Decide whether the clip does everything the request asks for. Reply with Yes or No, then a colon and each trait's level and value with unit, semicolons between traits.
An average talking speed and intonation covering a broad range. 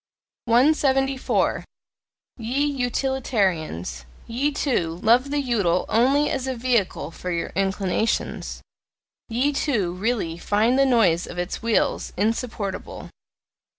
No: slow, 110 wpm; wide, 6.0 semitones